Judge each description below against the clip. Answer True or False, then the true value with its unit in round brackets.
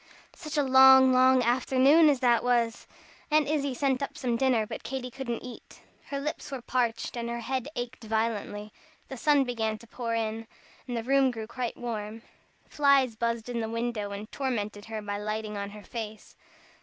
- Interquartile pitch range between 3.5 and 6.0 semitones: False (3.1 semitones)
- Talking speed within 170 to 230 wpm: True (180 wpm)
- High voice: True (240 Hz)